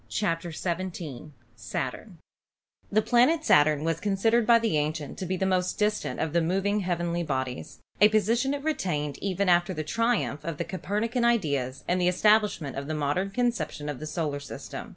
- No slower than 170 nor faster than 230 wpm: Yes, average, 175 wpm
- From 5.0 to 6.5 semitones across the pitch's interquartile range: Yes, wide, 5.6 semitones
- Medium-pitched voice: Yes, medium, 180 Hz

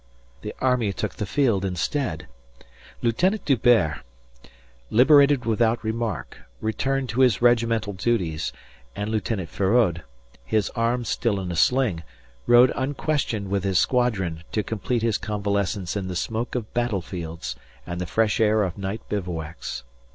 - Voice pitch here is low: Yes, low, 110 Hz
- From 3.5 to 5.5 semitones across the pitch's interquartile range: Yes, average, 4.1 semitones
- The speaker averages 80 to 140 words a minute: Yes, slow, 135 wpm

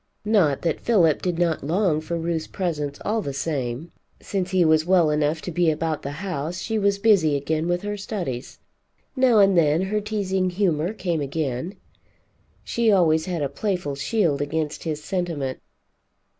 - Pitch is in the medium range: Yes, medium, 170 Hz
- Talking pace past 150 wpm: Yes, average, 170 wpm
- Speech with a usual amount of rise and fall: Yes, average, 4.2 semitones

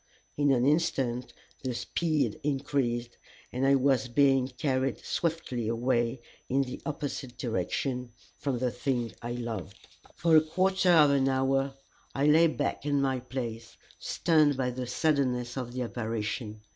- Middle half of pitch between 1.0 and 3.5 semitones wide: Yes, average, 2.9 semitones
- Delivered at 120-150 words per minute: Yes, average, 145 wpm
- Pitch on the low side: Yes, low, 130 Hz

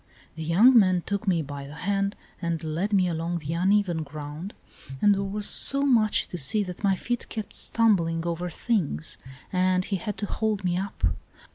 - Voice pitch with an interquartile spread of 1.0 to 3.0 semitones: No, average, 3.8 semitones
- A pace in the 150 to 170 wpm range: No, average, 185 wpm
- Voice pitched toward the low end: No, medium, 185 Hz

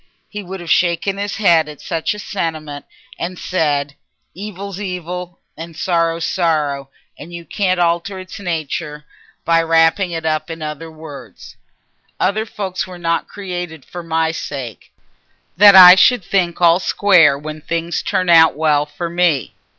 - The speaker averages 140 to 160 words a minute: Yes, average, 155 wpm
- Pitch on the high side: No, medium, 170 Hz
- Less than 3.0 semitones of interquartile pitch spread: Yes, narrow, 2.6 semitones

